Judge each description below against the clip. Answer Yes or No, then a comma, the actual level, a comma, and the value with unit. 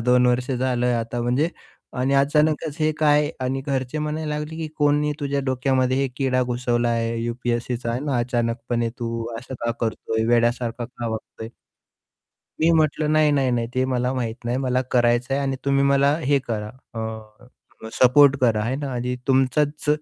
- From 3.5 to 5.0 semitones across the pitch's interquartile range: No, average, 2.9 semitones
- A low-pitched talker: Yes, low, 125 Hz